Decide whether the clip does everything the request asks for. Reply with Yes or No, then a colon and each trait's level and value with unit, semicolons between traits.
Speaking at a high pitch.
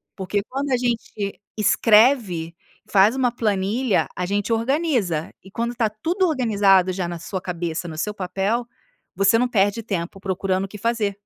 Yes: high, 205 Hz